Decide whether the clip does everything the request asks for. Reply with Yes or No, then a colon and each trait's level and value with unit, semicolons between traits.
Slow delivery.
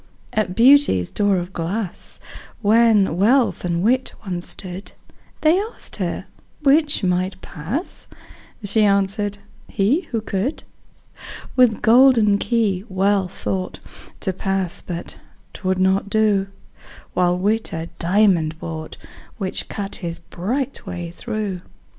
Yes: slow, 120 wpm